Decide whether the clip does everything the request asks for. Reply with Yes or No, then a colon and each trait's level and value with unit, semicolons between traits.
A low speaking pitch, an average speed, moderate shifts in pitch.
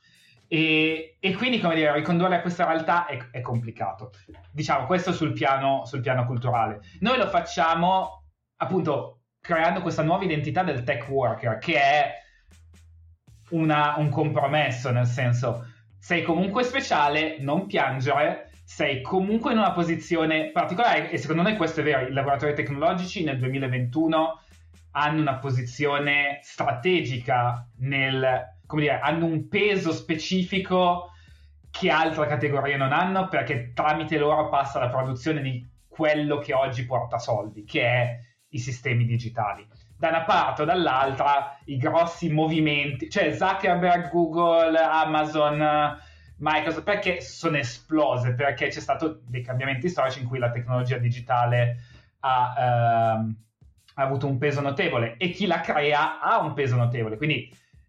No: medium, 145 Hz; average, 140 wpm; average, 4.8 semitones